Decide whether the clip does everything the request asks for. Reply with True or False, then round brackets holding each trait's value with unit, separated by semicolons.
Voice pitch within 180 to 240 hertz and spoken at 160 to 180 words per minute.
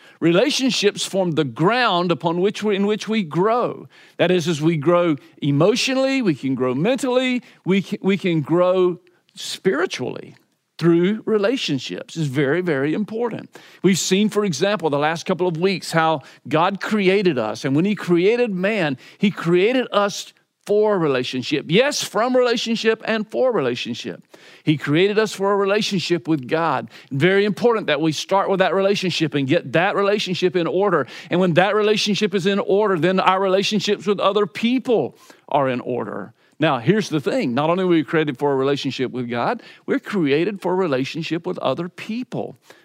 True (185 Hz; 170 wpm)